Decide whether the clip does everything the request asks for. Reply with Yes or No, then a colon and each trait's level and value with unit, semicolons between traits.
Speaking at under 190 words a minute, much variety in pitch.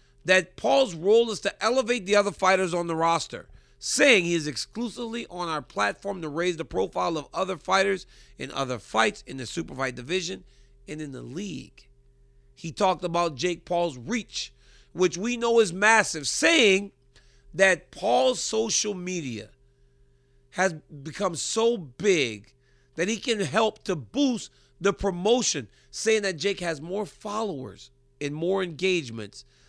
Yes: average, 150 wpm; wide, 7.2 semitones